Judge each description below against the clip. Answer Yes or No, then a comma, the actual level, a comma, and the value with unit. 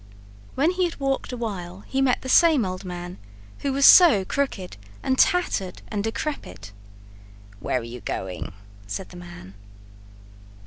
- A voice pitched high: Yes, high, 205 Hz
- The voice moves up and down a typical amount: No, wide, 7.7 semitones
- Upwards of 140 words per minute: Yes, average, 150 wpm